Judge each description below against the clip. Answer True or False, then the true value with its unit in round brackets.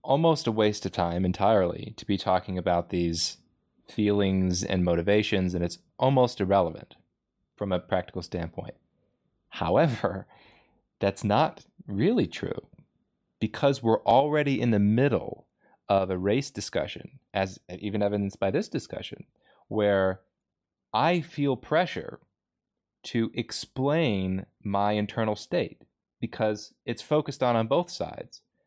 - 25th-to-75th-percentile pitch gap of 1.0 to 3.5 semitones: False (4.0 semitones)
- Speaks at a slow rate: True (125 wpm)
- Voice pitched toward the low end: True (105 Hz)